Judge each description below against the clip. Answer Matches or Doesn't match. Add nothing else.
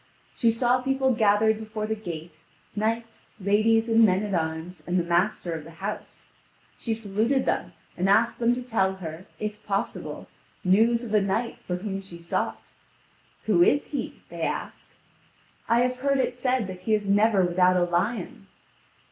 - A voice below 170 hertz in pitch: Doesn't match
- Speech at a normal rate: Matches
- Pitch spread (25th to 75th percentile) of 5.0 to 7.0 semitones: Doesn't match